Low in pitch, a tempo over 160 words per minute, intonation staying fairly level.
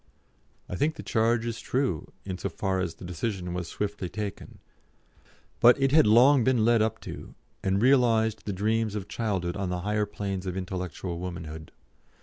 No: low, 105 Hz; average, 175 wpm; average, 3.8 semitones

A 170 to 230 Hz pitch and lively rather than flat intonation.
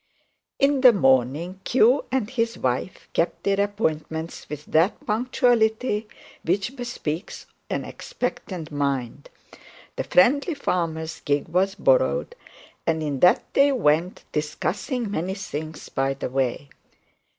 Yes: medium, 185 Hz; wide, 7.9 semitones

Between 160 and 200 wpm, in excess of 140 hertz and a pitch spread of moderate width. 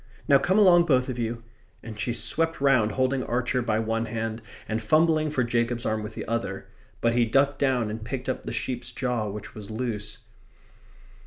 No: average, 190 wpm; low, 120 Hz; average, 3.1 semitones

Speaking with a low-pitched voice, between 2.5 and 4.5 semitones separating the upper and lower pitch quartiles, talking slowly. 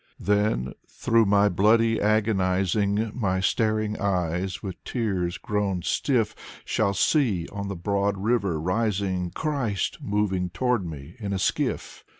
Yes: low, 100 Hz; average, 2.8 semitones; slow, 130 wpm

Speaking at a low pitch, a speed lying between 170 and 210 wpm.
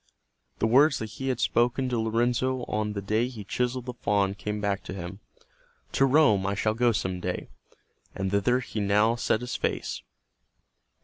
Yes: low, 110 Hz; average, 180 wpm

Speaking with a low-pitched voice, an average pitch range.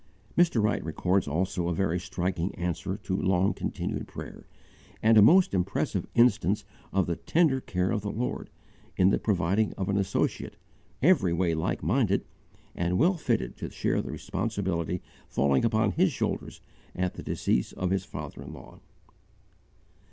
Yes: very low, 95 Hz; average, 3.6 semitones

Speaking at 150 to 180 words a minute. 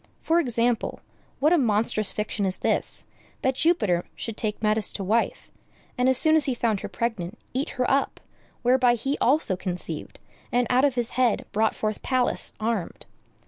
Yes: average, 175 wpm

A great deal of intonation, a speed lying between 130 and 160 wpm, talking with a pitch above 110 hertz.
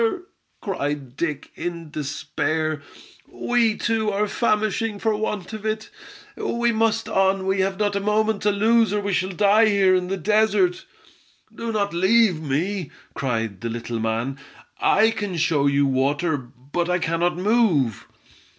Yes: wide, 6.1 semitones; average, 150 wpm; high, 190 Hz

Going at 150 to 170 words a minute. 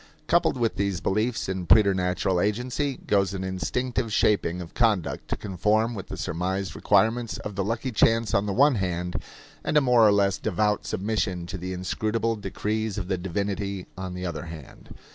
No: average, 180 wpm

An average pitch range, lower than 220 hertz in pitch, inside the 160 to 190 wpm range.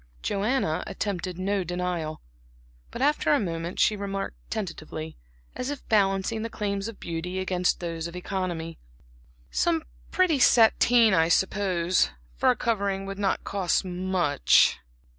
No: average, 3.5 semitones; high, 190 Hz; slow, 135 wpm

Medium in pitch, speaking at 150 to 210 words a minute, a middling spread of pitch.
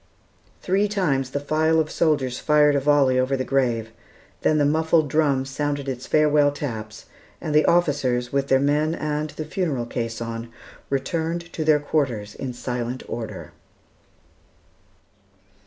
No: medium, 145 Hz; average, 140 wpm; average, 3.2 semitones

